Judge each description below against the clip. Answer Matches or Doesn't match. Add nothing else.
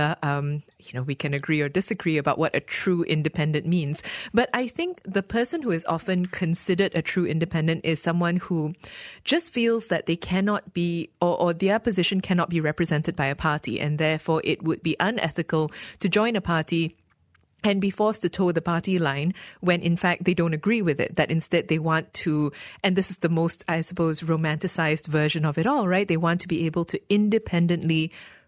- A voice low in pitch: Doesn't match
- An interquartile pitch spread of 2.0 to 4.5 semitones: Matches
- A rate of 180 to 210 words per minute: Matches